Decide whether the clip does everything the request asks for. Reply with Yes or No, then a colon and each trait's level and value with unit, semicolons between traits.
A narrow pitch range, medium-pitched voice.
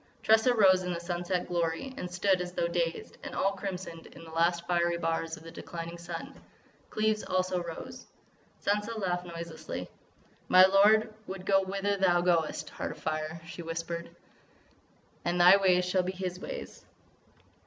Yes: narrow, 2.3 semitones; medium, 180 Hz